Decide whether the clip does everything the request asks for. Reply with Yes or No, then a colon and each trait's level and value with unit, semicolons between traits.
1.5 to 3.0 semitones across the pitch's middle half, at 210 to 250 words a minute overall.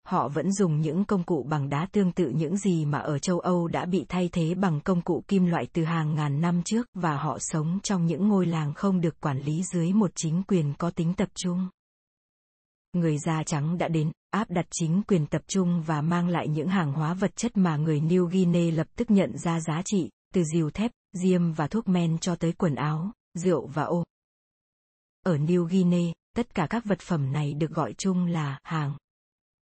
Yes: average, 2.7 semitones; average, 215 wpm